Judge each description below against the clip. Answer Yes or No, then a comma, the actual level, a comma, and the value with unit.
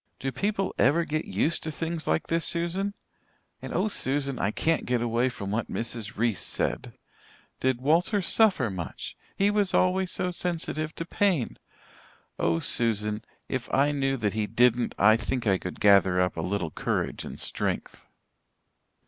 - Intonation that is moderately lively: No, wide, 7.5 semitones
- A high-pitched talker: No, low, 130 Hz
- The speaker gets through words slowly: No, average, 165 wpm